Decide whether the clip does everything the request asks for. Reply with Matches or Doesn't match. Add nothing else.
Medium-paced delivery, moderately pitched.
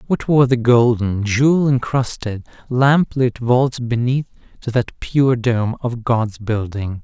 Doesn't match